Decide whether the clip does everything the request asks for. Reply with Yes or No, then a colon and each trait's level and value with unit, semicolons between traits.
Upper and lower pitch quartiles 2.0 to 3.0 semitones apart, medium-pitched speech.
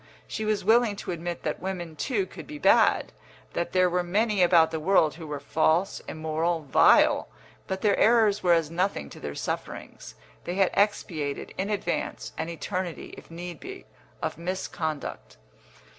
No: average, 3.7 semitones; medium, 175 Hz